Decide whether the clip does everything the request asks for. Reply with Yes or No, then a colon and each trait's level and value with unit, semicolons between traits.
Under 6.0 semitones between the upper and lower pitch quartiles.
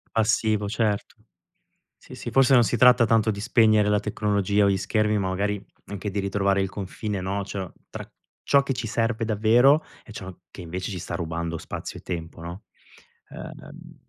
Yes: average, 2.7 semitones